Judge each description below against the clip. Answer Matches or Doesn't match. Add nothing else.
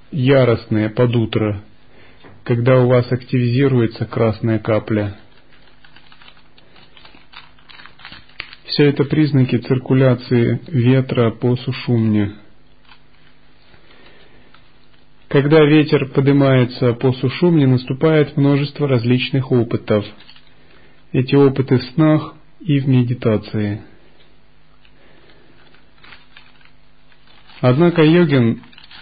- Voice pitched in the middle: Doesn't match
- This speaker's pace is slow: Matches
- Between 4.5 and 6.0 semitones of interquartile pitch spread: Doesn't match